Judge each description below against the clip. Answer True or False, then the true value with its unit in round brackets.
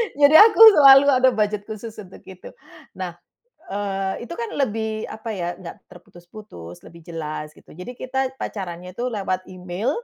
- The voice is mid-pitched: False (205 Hz)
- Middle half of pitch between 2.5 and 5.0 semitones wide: False (5.4 semitones)